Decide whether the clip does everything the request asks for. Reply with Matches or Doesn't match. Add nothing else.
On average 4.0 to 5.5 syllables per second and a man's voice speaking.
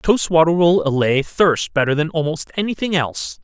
Matches